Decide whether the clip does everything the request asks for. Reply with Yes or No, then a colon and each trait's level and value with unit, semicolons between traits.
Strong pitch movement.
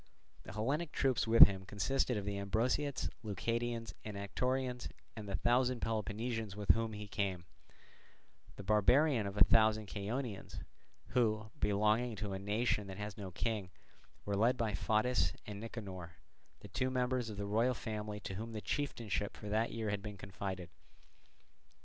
No: average, 2.8 semitones